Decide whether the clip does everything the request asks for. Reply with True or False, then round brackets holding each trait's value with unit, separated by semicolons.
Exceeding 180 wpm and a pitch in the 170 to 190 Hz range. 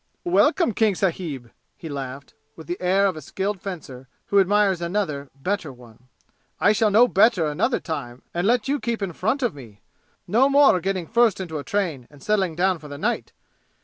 True (190 wpm; 185 Hz)